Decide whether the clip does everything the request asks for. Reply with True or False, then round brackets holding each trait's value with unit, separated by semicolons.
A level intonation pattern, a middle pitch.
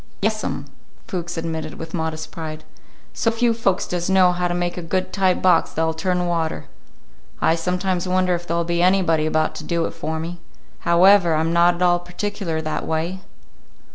True (2.1 semitones; 175 Hz)